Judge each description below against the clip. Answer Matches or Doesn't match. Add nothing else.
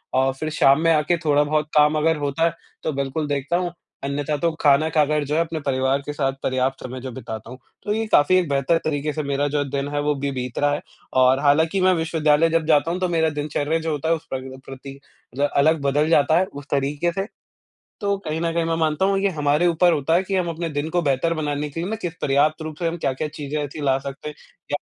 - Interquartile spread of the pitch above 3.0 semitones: Doesn't match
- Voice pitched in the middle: Matches